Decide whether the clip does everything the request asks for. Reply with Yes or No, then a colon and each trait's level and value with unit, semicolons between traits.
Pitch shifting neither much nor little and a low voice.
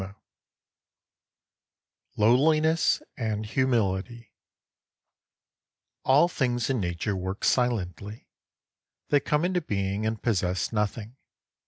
Yes: average, 4.8 semitones; low, 115 Hz